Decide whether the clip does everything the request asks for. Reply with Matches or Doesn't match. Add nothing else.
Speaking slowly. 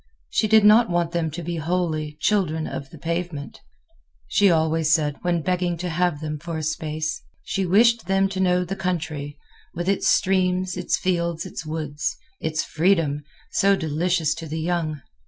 Doesn't match